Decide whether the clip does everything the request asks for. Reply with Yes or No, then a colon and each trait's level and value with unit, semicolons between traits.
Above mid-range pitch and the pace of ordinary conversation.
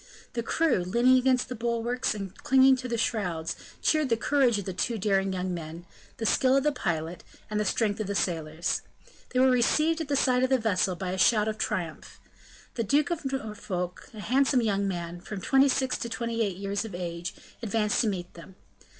No: high, 215 Hz; fast, 210 wpm